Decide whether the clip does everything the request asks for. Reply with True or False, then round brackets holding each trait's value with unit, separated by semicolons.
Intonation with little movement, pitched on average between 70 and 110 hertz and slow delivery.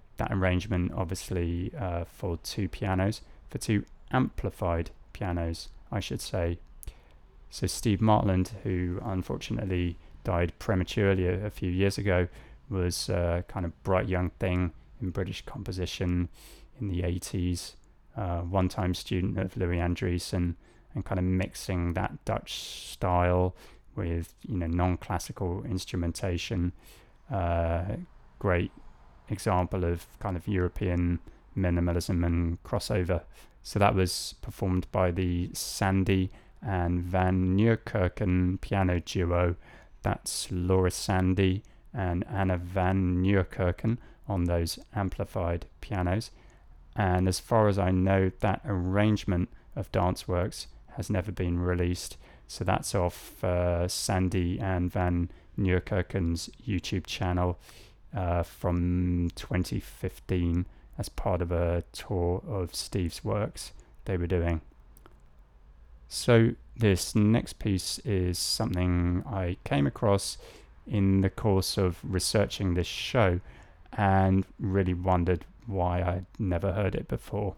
True (1.8 semitones; 90 Hz; 120 wpm)